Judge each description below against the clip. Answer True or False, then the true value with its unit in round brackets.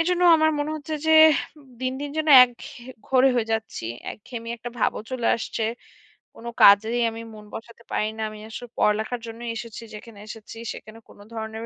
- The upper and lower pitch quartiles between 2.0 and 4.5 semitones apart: True (2.6 semitones)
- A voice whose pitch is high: True (230 Hz)